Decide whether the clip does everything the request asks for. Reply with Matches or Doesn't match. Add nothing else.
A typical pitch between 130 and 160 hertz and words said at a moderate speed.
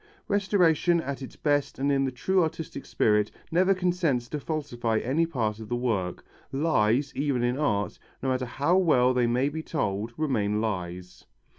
Matches